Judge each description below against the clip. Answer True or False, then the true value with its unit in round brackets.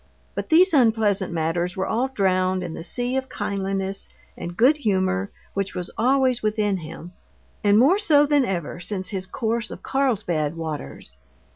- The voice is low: False (200 Hz)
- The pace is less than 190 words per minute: True (160 wpm)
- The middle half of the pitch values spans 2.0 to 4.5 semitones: False (5.2 semitones)